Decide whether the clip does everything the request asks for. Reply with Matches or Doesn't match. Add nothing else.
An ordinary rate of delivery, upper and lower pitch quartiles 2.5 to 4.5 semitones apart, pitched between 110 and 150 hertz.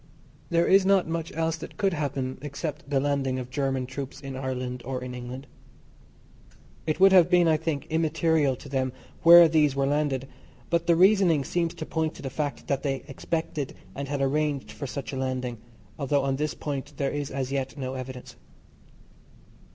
Matches